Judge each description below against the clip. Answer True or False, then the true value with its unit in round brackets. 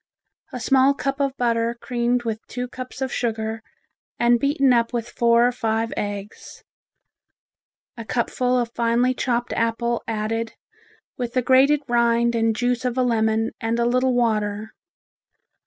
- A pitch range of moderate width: False (1.7 semitones)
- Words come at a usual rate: True (150 wpm)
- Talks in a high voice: True (235 Hz)